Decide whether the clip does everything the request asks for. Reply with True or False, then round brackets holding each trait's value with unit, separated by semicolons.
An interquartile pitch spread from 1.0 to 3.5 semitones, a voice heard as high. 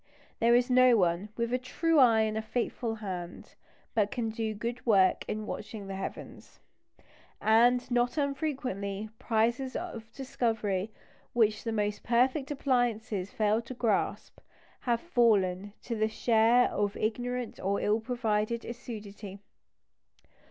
True (2.8 semitones; 225 Hz)